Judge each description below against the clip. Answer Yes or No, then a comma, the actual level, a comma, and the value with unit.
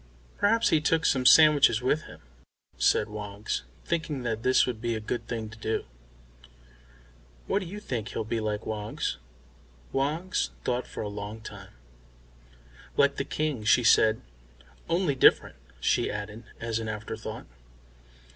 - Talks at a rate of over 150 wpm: No, average, 145 wpm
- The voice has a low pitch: Yes, low, 120 Hz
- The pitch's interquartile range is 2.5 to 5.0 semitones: No, wide, 5.5 semitones